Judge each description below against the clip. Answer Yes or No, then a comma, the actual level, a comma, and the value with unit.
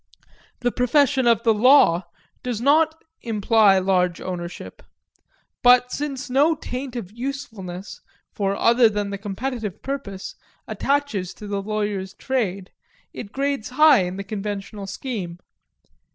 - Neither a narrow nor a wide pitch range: Yes, average, 5.0 semitones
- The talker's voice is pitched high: Yes, high, 220 Hz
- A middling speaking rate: No, slow, 125 wpm